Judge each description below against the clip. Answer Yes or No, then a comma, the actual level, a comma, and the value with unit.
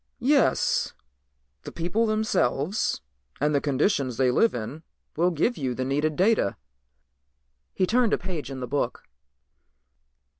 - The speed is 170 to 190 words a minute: No, slow, 135 wpm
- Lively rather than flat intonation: Yes, wide, 8.1 semitones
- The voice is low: No, medium, 155 Hz